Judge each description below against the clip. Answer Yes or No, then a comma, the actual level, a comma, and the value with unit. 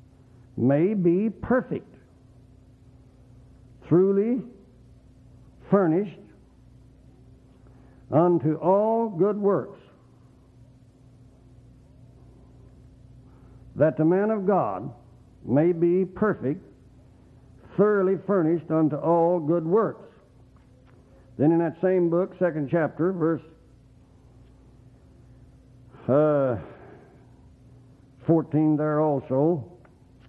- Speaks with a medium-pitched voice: No, low, 130 Hz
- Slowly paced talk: Yes, slow, 70 wpm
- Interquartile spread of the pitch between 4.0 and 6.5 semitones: Yes, wide, 5.5 semitones